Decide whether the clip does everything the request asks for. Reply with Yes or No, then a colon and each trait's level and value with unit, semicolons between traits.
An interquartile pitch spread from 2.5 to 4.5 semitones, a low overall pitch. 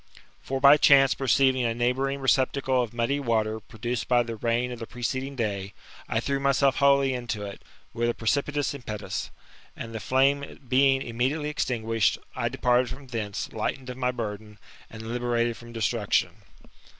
Yes: average, 2.9 semitones; low, 125 Hz